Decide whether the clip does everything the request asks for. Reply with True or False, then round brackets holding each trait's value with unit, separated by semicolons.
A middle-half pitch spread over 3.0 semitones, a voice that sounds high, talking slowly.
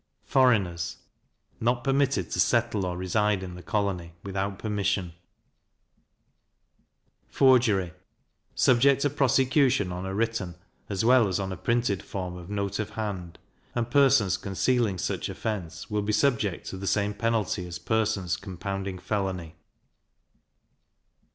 False (4.0 semitones; 100 Hz; 130 wpm)